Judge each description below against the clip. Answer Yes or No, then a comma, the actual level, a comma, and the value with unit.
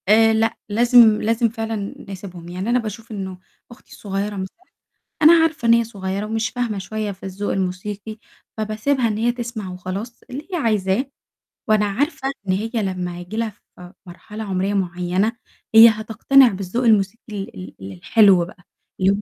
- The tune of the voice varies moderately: Yes, average, 3.3 semitones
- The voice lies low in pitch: No, high, 210 Hz